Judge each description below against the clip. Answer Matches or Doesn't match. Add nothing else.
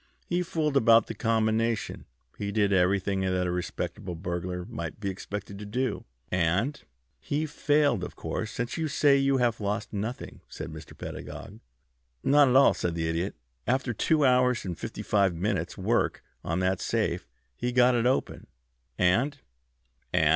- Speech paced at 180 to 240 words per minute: Doesn't match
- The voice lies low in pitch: Matches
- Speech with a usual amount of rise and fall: Doesn't match